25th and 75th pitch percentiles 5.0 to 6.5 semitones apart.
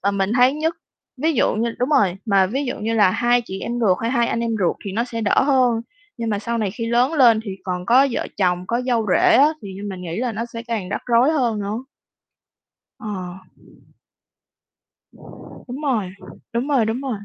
No: average, 3.7 semitones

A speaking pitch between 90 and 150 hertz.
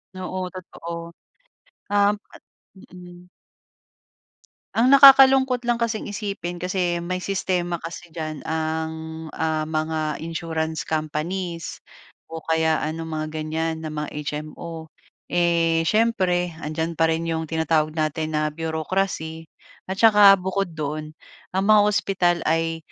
No: medium, 165 Hz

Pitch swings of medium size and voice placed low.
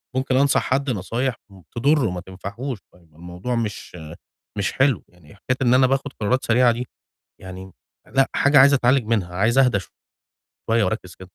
No: wide, 5.7 semitones; low, 115 Hz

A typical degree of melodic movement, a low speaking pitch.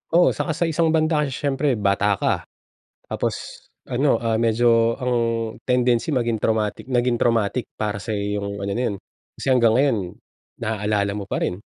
Yes: average, 3.9 semitones; low, 115 Hz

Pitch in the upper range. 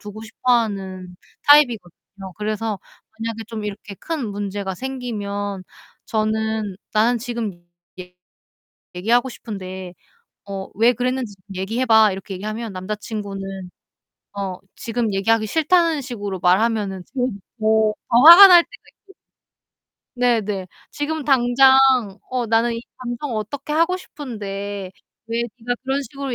Yes: high, 220 Hz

